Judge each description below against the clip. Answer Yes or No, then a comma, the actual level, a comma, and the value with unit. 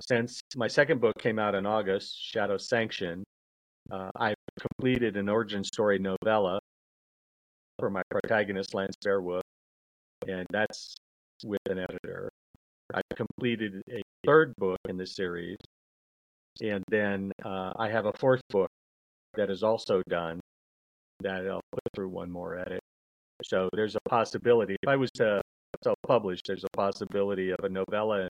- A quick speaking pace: No, average, 145 wpm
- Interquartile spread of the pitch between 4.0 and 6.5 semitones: No, average, 3.1 semitones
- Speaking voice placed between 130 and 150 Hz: No, low, 100 Hz